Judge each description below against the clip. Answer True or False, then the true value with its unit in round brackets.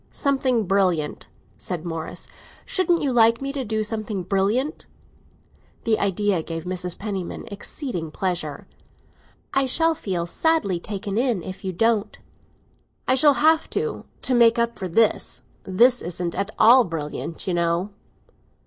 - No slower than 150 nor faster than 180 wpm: False (140 wpm)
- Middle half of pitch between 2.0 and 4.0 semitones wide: False (5.6 semitones)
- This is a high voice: True (205 Hz)